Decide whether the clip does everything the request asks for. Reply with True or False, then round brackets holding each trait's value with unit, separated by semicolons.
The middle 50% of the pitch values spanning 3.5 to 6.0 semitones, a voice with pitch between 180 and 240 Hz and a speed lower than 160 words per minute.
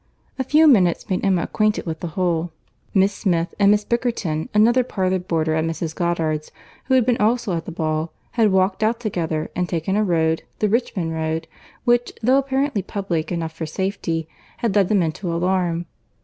False (4.6 semitones; 185 Hz; 185 wpm)